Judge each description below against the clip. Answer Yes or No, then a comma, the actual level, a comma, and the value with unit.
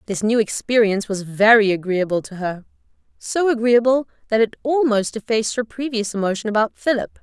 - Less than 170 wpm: Yes, average, 160 wpm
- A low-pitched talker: No, high, 220 Hz